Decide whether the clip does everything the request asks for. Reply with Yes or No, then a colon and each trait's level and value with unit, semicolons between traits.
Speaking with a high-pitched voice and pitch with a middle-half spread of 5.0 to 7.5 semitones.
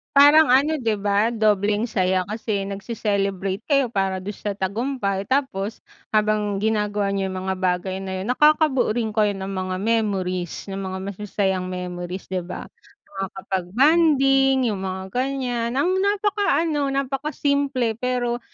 Yes: high, 210 Hz; wide, 5.5 semitones